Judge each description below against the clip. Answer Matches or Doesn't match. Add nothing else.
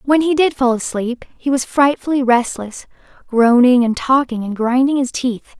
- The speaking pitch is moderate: Doesn't match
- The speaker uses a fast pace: Doesn't match